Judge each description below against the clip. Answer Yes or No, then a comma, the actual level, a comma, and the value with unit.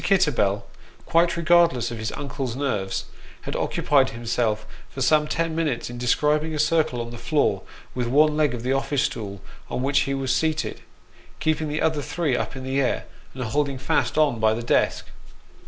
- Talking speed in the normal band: Yes, average, 185 wpm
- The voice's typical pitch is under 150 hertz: Yes, low, 135 Hz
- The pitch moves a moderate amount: Yes, average, 4.1 semitones